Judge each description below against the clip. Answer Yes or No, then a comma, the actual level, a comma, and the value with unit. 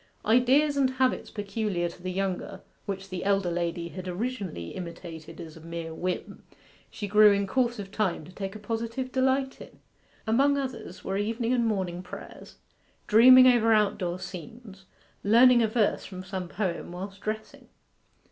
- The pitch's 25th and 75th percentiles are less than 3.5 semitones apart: No, average, 4.5 semitones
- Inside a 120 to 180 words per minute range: Yes, average, 165 wpm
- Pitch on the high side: Yes, high, 200 Hz